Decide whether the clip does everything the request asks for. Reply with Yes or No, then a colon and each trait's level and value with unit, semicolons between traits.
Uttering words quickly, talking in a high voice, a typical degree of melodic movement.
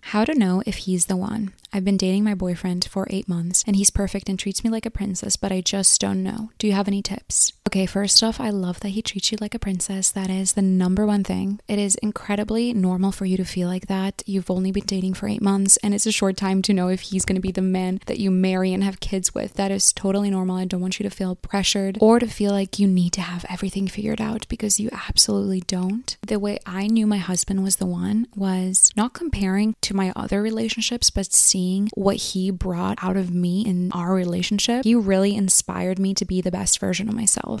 No: fast, 245 wpm; high, 195 Hz; narrow, 1.8 semitones